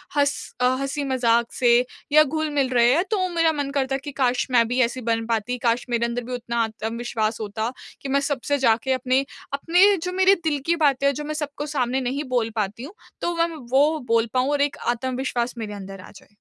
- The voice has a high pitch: Yes, very high, 255 Hz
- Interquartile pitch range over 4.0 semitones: No, average, 3.5 semitones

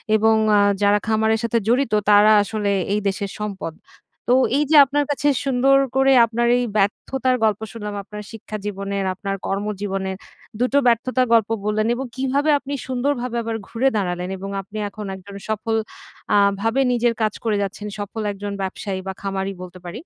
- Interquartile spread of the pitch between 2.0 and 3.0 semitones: No, average, 3.5 semitones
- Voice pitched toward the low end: No, high, 215 Hz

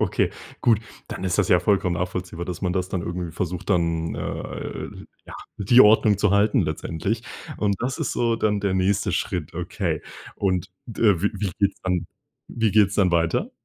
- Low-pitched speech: Yes, very low, 95 Hz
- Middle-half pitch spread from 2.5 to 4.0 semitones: Yes, average, 2.8 semitones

